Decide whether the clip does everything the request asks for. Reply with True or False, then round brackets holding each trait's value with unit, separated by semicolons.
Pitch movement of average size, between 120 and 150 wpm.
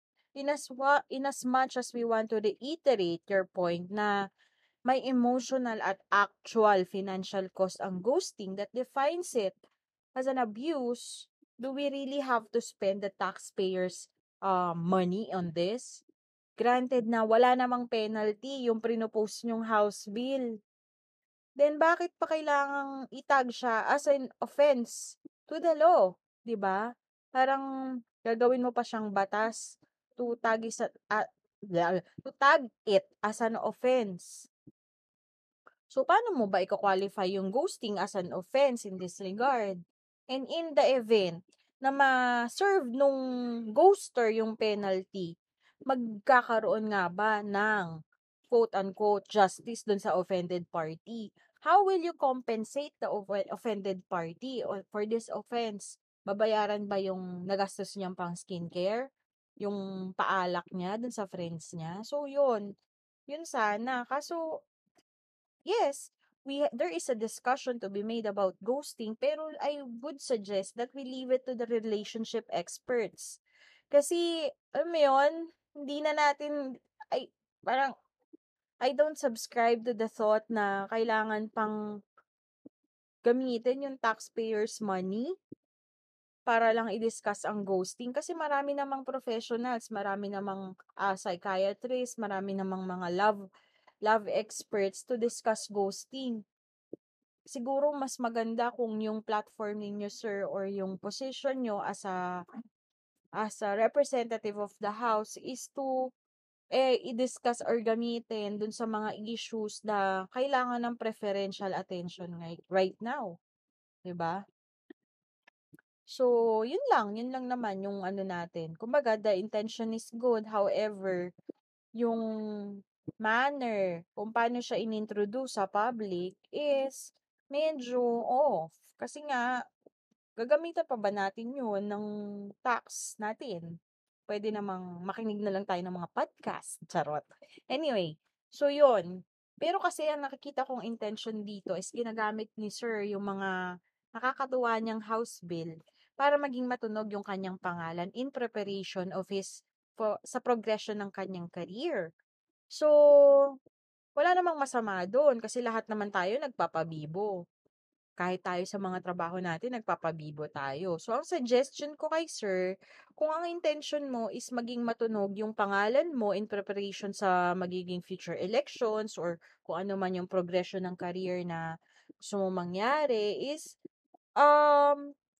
True (5.0 semitones; 130 wpm)